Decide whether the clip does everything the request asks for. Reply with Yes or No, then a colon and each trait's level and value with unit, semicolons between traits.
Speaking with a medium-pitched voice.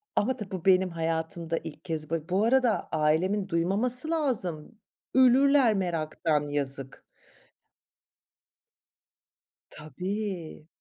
Yes: medium, 180 Hz